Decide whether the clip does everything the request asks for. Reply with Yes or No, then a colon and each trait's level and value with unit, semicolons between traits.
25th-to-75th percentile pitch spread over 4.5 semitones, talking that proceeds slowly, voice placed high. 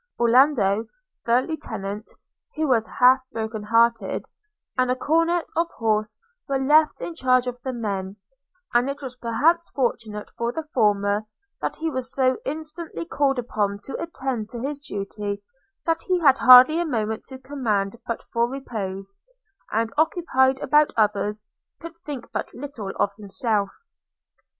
No: average, 5.1 semitones; average, 150 wpm; very high, 250 Hz